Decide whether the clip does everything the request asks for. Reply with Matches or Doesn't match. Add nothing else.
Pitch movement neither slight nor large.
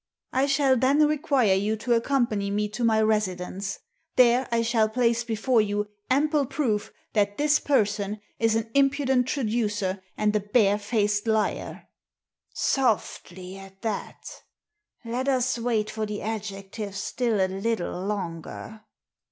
Matches